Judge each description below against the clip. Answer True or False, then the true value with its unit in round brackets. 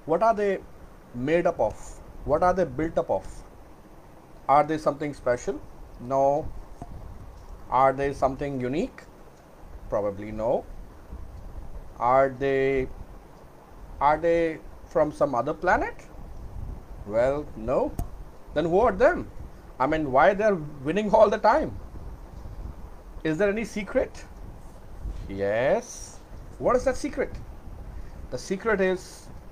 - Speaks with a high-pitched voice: False (135 Hz)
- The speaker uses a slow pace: True (115 wpm)